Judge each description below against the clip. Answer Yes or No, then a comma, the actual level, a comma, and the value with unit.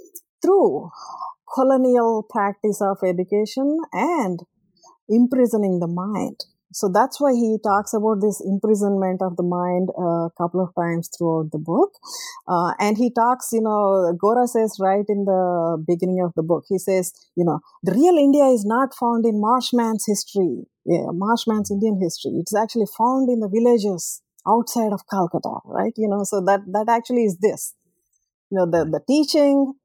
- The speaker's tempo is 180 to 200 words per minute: No, average, 165 wpm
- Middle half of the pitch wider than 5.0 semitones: No, average, 4.5 semitones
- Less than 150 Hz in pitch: No, high, 210 Hz